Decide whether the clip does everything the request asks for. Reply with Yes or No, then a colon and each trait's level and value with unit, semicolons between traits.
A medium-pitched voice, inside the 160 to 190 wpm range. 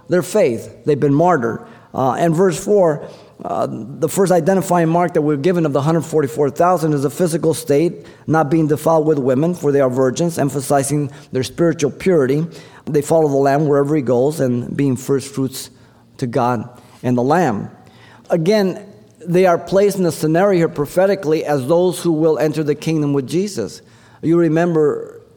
Yes: medium, 155 Hz; average, 170 wpm